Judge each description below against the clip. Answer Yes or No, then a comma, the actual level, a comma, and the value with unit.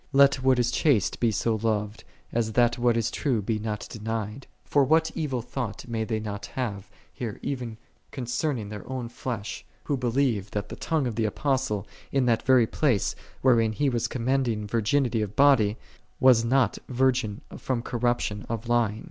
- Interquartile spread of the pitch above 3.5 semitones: No, average, 3.2 semitones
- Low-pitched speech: Yes, low, 120 Hz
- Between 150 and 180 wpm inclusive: Yes, average, 175 wpm